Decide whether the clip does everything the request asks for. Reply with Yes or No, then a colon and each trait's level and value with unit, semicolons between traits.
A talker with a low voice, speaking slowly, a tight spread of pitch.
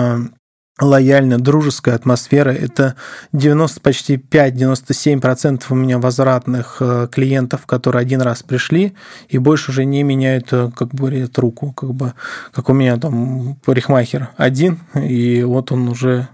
No: low, 130 Hz; average, 130 wpm; narrow, 1.9 semitones